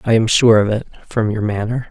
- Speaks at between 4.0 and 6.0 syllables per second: Yes, 5.6 syllables/s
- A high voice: No, low, 110 Hz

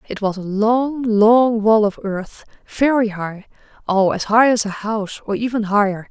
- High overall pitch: Yes, high, 215 Hz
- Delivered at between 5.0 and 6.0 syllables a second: No, 4.4 syllables/s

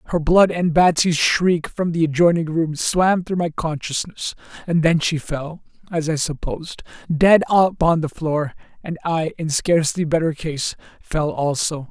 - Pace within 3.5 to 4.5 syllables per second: Yes, 4.4 syllables/s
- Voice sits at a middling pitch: Yes, medium, 160 Hz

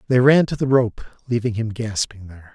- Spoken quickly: Yes, fast, 210 wpm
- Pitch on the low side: Yes, low, 115 Hz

